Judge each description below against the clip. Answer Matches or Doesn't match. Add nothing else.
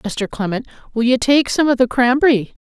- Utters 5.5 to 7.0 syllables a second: Doesn't match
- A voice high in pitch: Matches